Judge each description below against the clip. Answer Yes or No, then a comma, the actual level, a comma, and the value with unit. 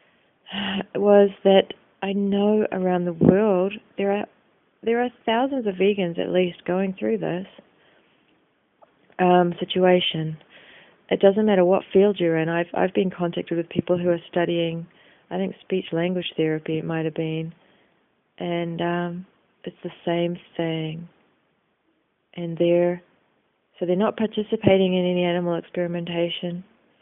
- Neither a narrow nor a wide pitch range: No, narrow, 2.3 semitones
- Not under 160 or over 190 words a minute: No, average, 140 wpm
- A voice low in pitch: No, medium, 180 Hz